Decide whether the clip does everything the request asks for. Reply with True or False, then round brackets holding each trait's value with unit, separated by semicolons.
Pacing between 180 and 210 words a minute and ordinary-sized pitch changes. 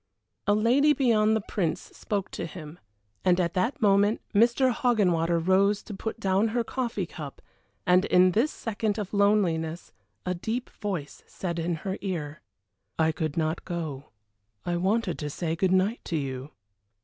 False (160 wpm; 4.4 semitones)